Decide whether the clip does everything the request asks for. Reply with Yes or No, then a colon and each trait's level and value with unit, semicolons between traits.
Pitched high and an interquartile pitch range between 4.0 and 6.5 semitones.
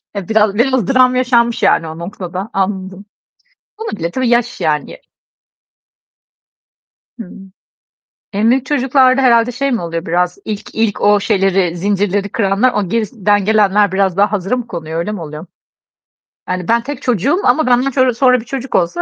Yes: high, 210 Hz; average, 4.7 semitones